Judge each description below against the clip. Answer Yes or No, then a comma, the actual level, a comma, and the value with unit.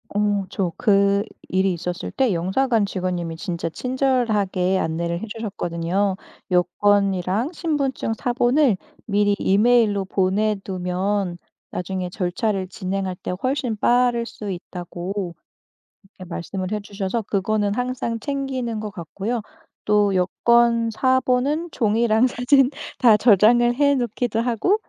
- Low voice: No, high, 205 Hz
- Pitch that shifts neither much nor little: Yes, average, 4.2 semitones